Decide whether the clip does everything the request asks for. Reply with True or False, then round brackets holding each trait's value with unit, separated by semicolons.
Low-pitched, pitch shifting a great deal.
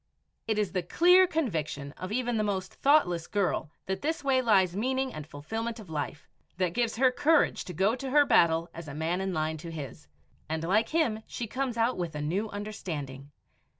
False (200 Hz; 7.1 semitones)